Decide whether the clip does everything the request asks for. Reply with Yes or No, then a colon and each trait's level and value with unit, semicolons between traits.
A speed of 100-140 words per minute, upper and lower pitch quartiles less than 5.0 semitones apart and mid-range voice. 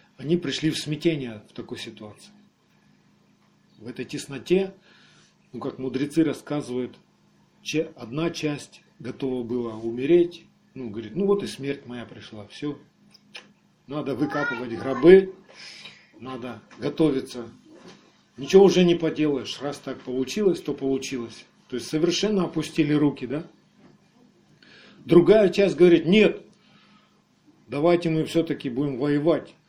No: average, 115 wpm; average, 5.3 semitones; medium, 150 Hz